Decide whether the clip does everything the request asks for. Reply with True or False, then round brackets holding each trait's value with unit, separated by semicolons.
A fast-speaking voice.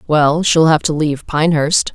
False (185 wpm)